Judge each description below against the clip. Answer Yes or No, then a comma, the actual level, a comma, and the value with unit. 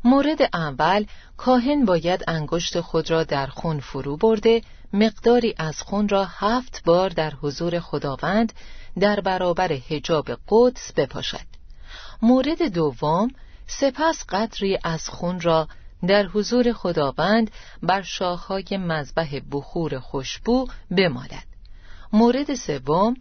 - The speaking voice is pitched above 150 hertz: Yes, medium, 185 Hz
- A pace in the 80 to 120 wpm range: Yes, average, 110 wpm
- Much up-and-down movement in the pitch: Yes, wide, 6.0 semitones